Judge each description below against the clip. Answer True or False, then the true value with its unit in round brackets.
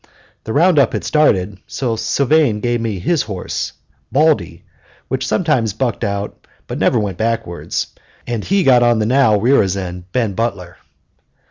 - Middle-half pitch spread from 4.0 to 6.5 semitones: True (5.1 semitones)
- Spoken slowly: False (150 wpm)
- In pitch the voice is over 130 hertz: False (115 Hz)